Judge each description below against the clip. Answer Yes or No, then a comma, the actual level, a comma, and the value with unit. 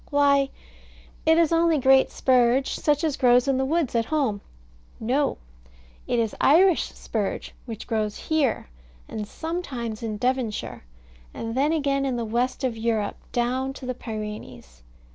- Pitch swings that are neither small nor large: Yes, average, 3.9 semitones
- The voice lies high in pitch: Yes, very high, 255 Hz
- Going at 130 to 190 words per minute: Yes, average, 150 wpm